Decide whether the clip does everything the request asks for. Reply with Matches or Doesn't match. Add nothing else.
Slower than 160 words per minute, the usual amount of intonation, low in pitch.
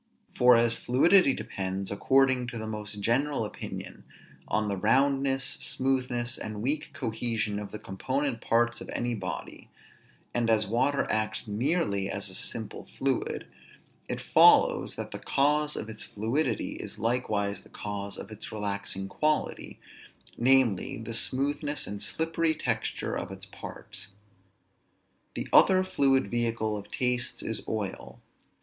Matches